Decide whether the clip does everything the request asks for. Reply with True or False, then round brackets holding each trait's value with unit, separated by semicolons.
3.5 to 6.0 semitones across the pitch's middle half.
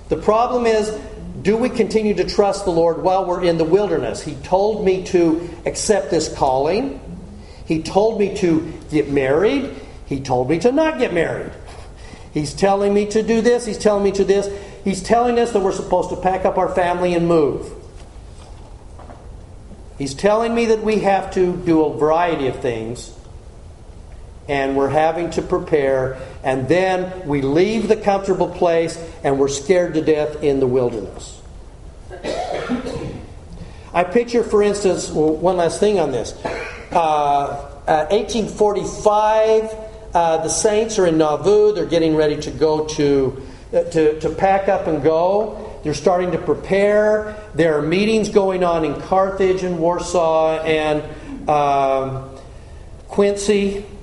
True (5.2 semitones)